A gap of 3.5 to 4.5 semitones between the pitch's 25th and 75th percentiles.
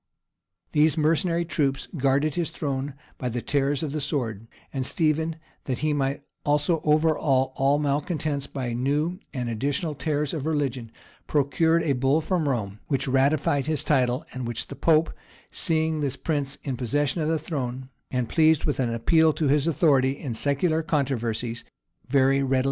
No: average, 2.9 semitones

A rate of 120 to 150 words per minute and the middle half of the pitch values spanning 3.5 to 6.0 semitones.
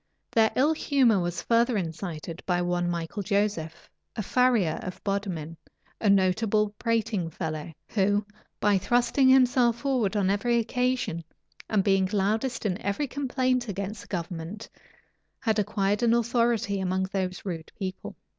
Yes: average, 140 wpm; average, 4.3 semitones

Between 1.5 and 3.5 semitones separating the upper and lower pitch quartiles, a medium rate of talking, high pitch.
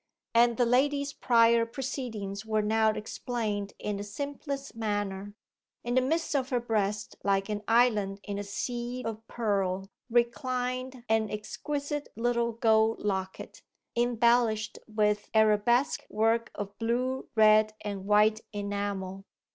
No: average, 2.8 semitones; slow, 130 wpm; high, 225 Hz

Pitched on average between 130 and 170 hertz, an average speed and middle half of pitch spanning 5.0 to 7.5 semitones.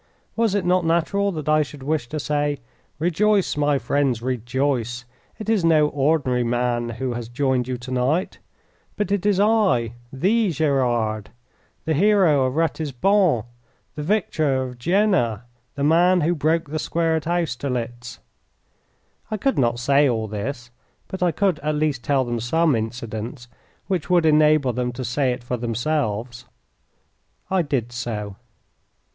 Yes: medium, 140 Hz; average, 150 wpm; wide, 5.4 semitones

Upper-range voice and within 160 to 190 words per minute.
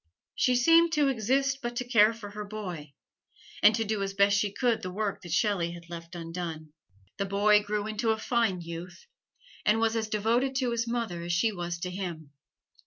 No: high, 210 Hz; average, 200 wpm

